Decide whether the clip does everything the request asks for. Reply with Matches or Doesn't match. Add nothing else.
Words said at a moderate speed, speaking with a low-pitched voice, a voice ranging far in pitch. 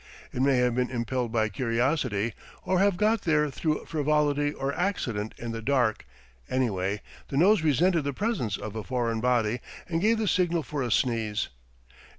Matches